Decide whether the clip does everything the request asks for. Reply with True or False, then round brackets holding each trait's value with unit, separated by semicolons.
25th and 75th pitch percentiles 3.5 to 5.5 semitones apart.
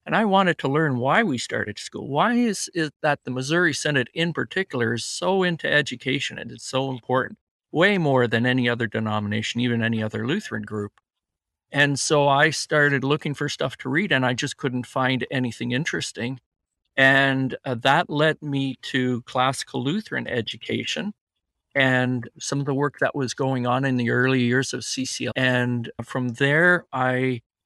False (2.8 semitones)